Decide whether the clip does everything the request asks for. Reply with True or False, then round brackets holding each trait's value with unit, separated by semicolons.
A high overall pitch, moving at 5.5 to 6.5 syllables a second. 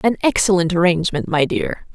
False (180 Hz; 5.7 syllables/s)